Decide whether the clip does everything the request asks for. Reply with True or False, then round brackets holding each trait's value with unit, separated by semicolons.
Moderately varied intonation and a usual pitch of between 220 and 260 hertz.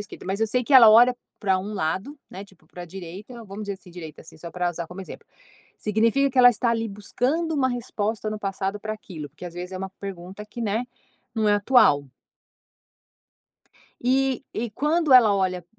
False (4.6 semitones; 205 Hz)